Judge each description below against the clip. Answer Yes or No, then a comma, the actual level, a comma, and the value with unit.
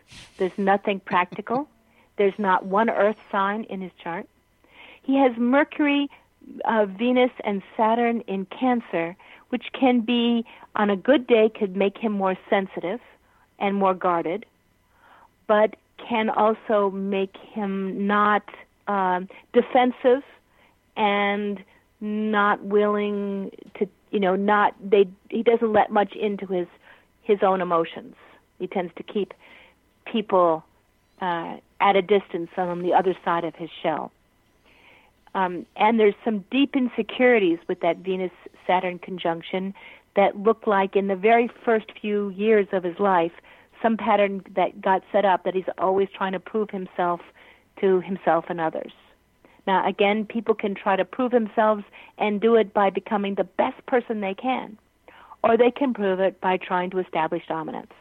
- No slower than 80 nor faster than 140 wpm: No, average, 150 wpm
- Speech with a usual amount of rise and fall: Yes, average, 3.1 semitones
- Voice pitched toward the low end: No, high, 200 Hz